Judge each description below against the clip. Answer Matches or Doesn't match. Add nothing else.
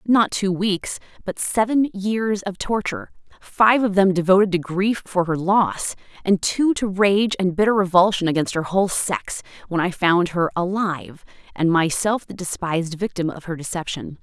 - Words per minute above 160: Matches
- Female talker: Matches